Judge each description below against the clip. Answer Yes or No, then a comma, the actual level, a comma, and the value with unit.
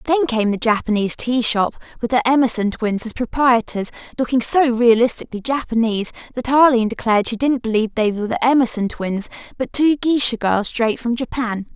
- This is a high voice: Yes, high, 235 Hz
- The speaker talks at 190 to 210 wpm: No, average, 175 wpm